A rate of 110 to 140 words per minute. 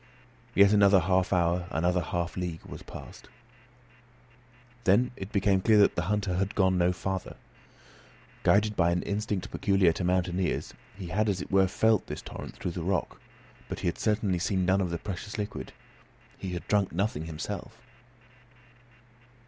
No: average, 165 wpm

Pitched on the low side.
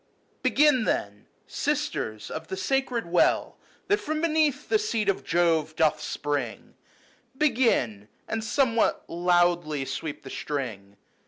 No: medium, 175 Hz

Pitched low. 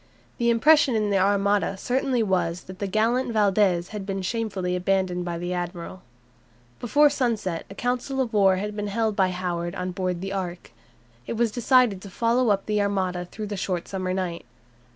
No: high, 195 Hz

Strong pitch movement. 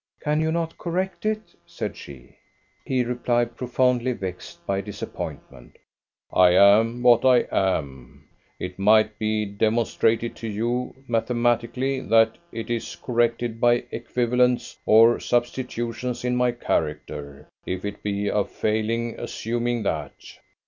No: average, 3.1 semitones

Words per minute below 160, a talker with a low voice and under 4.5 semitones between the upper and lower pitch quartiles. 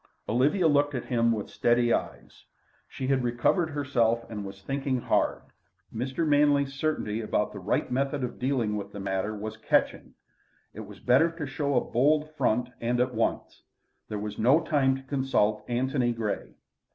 No: average, 170 wpm; low, 125 Hz; average, 4.1 semitones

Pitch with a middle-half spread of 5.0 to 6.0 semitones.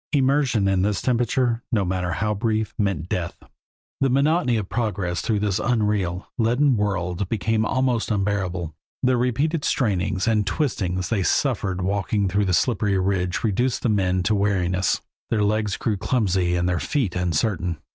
No: average, 4.0 semitones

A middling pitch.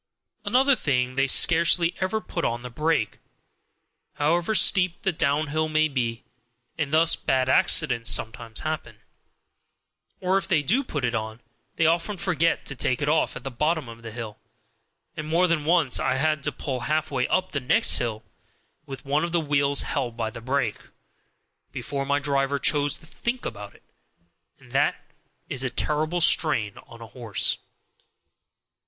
Yes: medium, 145 Hz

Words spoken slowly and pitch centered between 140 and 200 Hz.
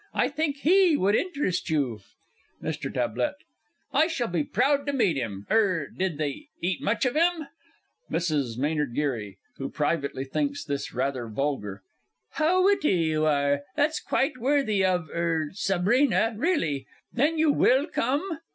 No: average, 150 wpm; high, 190 Hz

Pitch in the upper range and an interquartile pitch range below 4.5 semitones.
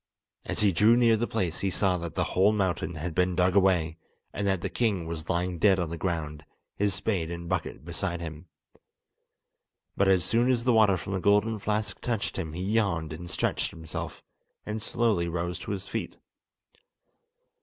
No: very low, 95 Hz; average, 3.3 semitones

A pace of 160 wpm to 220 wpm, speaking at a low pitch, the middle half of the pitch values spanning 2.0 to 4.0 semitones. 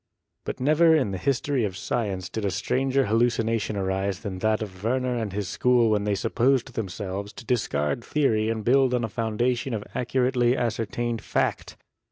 Yes: average, 180 wpm; low, 115 Hz; average, 3.6 semitones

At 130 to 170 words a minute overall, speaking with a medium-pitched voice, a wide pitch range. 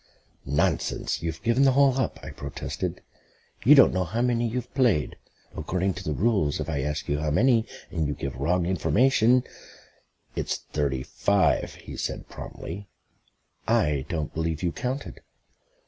No: average, 160 wpm; very low, 95 Hz; wide, 8.2 semitones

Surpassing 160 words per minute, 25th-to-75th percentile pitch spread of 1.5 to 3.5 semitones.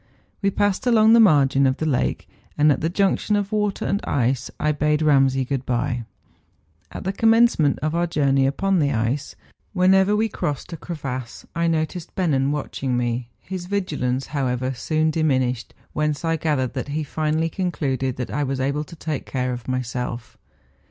No: average, 180 wpm; average, 4.9 semitones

